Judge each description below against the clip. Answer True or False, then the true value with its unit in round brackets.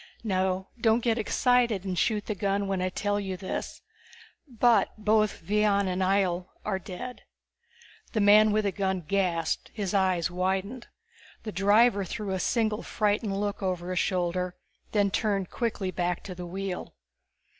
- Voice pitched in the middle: False (195 Hz)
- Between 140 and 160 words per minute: True (155 wpm)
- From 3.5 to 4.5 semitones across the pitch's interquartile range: False (2.4 semitones)